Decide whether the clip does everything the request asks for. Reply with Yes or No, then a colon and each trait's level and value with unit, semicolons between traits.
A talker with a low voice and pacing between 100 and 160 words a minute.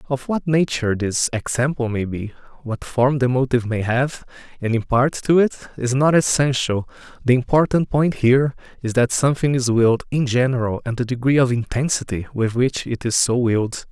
No: low, 125 Hz; average, 180 wpm